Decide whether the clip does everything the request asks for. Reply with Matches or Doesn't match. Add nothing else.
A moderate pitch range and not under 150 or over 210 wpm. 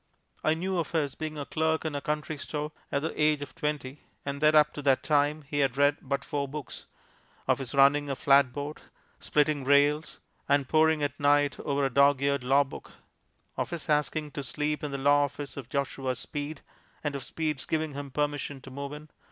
Doesn't match